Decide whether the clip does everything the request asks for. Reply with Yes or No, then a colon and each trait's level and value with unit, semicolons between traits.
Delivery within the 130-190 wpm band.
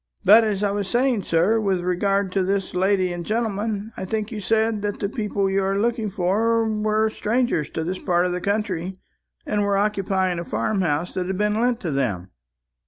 No: fast, 205 wpm